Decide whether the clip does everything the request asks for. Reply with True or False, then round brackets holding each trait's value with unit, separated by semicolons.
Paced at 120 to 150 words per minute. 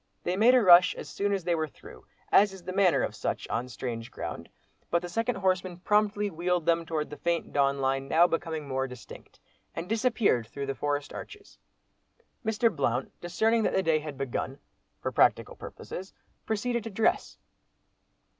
False (175 wpm)